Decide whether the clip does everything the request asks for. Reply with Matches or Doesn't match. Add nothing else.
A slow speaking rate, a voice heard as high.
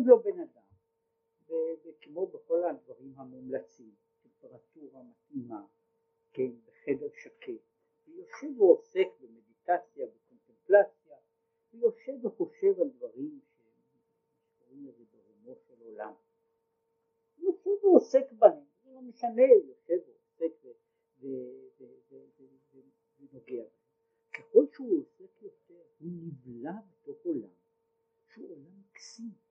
Matches